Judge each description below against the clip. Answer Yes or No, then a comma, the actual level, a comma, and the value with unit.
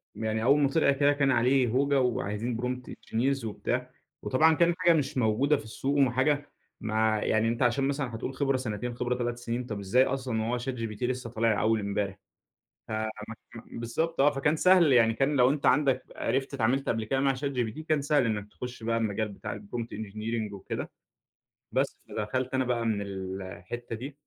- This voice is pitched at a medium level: No, low, 125 Hz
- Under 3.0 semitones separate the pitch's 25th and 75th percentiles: No, average, 3.6 semitones